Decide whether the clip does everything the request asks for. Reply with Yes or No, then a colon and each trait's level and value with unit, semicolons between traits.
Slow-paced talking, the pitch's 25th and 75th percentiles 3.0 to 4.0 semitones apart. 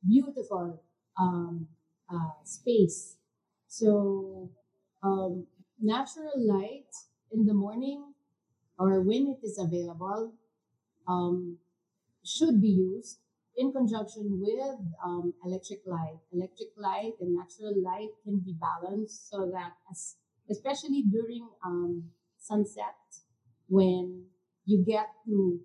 Yes: slow, 105 wpm; average, 3.4 semitones